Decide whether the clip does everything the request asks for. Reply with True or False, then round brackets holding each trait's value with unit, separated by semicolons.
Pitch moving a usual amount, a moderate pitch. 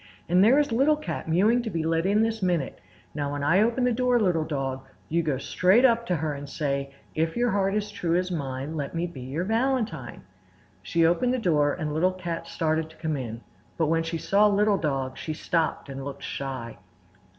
False (6.4 semitones; 165 Hz)